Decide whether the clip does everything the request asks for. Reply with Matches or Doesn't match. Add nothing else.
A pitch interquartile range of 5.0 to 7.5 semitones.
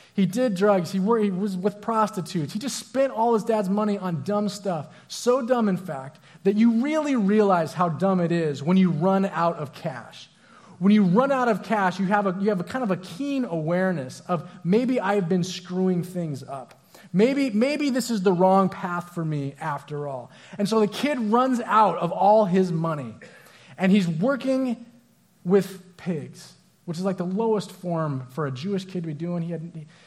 Doesn't match